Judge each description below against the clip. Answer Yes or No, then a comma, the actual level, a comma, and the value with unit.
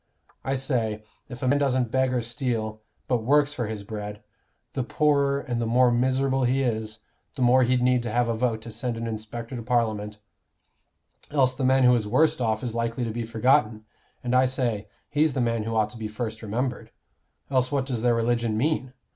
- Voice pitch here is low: Yes, low, 120 Hz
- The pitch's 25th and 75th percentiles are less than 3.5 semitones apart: Yes, narrow, 2.6 semitones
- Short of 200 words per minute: No, fast, 205 wpm